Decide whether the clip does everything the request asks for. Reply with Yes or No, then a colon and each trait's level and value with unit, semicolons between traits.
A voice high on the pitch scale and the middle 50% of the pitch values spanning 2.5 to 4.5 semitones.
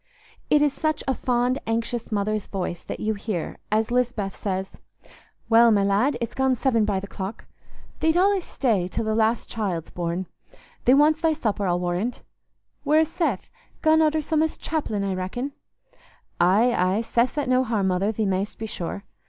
No: high, 225 Hz; average, 5.1 semitones